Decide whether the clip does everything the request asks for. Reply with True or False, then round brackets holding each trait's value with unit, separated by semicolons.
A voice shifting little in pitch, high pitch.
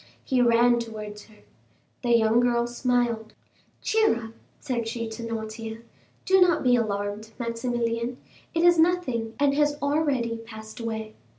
True (2.2 semitones; 235 Hz)